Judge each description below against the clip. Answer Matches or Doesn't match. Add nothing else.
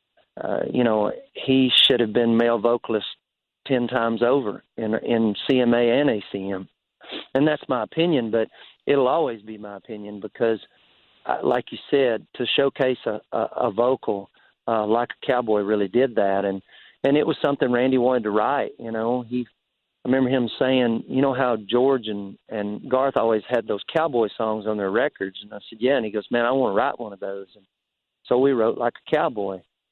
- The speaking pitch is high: Doesn't match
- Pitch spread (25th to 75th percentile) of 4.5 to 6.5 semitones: Doesn't match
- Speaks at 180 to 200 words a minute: Matches